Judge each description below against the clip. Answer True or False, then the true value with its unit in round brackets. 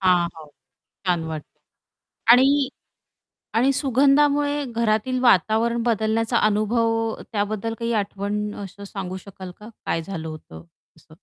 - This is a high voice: True (215 Hz)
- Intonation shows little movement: False (3.9 semitones)